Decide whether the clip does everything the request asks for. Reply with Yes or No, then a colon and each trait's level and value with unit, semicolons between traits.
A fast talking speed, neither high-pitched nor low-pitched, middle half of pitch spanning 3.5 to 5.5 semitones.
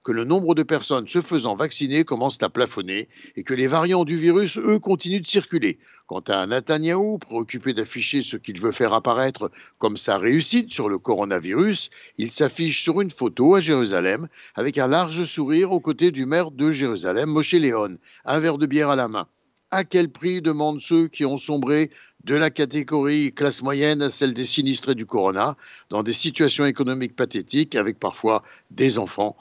Yes: fast, 185 wpm; medium, 150 Hz; average, 4.1 semitones